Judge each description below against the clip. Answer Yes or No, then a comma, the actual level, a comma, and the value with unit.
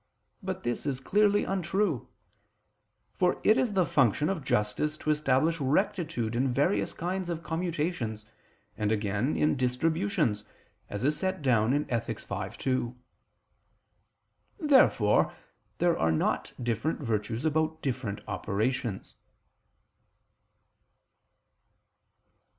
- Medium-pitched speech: Yes, medium, 150 Hz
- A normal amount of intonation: No, wide, 6.7 semitones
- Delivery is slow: Yes, slow, 110 wpm